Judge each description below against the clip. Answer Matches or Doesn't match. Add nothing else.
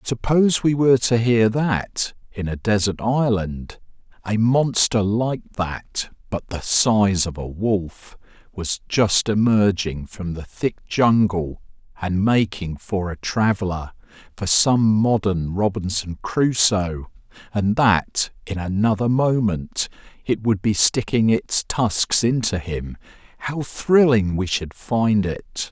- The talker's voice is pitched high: Doesn't match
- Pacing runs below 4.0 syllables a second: Matches